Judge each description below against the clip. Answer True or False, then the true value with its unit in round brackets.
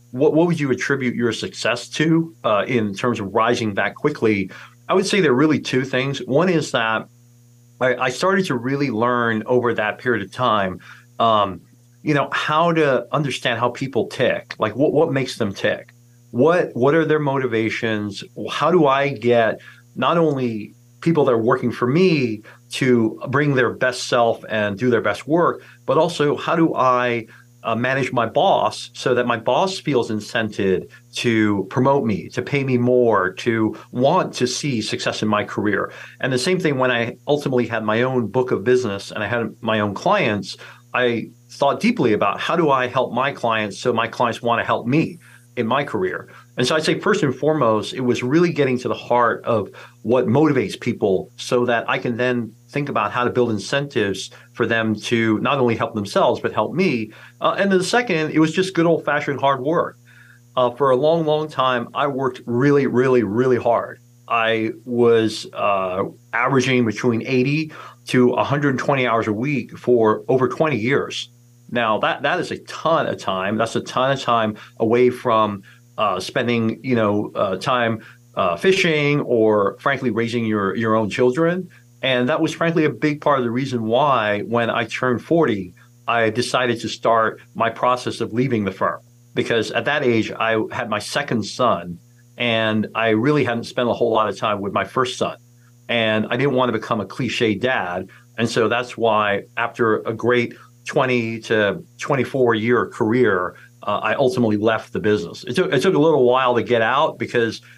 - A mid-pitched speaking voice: False (120 Hz)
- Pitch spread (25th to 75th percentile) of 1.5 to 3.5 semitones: True (2.8 semitones)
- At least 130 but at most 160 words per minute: False (190 wpm)